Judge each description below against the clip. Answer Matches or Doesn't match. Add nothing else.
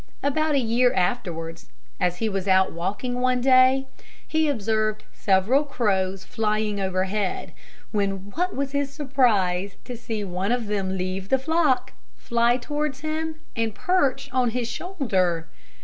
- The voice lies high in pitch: Matches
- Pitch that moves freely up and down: Matches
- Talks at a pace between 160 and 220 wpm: Doesn't match